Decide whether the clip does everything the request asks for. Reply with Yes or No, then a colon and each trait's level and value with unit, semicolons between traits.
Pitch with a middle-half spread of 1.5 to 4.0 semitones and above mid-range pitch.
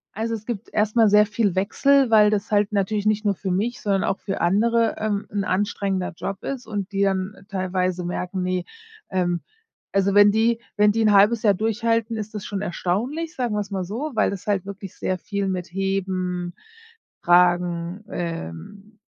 Yes: narrow, 2.5 semitones; high, 200 Hz